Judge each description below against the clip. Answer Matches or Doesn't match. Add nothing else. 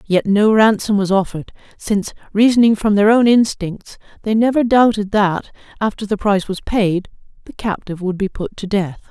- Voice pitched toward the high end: Matches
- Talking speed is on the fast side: Doesn't match